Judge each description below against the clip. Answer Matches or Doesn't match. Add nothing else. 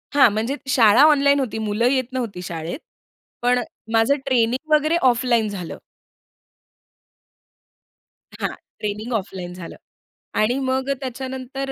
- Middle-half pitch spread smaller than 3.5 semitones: Doesn't match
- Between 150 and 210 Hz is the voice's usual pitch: Doesn't match